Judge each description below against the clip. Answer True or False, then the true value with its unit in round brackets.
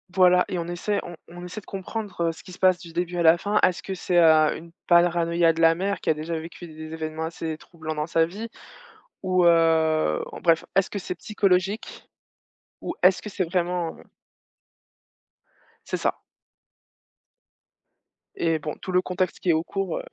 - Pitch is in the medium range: True (170 Hz)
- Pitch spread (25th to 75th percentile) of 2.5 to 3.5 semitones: False (2.1 semitones)